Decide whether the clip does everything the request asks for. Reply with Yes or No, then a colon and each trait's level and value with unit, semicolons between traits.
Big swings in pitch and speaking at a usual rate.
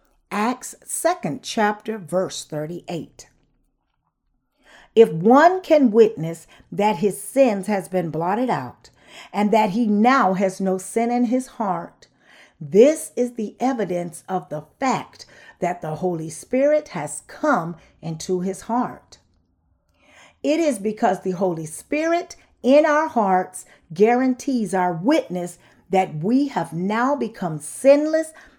No: wide, 6.4 semitones; slow, 130 wpm